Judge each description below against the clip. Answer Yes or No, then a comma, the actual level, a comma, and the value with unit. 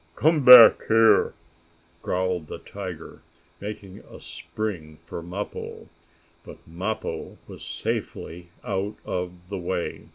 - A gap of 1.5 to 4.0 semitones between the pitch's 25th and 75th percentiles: Yes, average, 3.4 semitones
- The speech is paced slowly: Yes, slow, 110 wpm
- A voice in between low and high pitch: No, very low, 95 Hz